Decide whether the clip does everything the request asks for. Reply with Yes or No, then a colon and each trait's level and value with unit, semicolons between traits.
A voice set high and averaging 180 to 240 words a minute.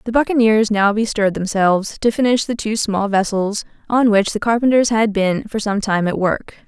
Yes: high, 215 Hz; average, 200 wpm